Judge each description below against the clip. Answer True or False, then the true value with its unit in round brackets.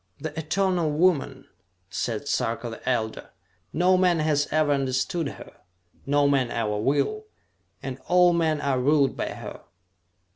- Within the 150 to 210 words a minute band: False (140 wpm)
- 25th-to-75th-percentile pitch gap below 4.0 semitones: False (4.4 semitones)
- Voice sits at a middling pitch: True (145 Hz)